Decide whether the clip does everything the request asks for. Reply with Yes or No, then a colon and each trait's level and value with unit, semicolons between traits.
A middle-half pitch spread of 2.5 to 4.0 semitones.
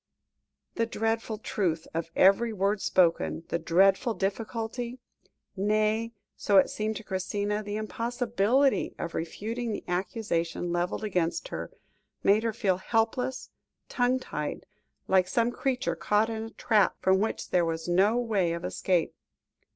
Yes: average, 3.7 semitones